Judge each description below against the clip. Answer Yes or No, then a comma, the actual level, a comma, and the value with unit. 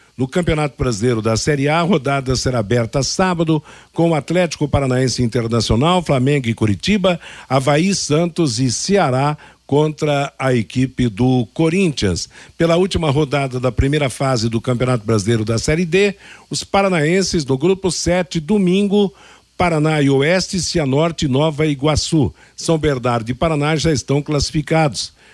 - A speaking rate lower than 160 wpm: Yes, average, 140 wpm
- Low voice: No, medium, 145 Hz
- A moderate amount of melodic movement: Yes, average, 4.8 semitones